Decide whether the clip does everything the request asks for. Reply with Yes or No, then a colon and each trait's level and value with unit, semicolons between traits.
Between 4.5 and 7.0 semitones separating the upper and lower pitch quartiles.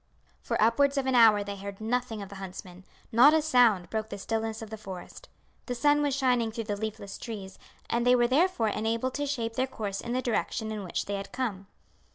No: average, 3.6 semitones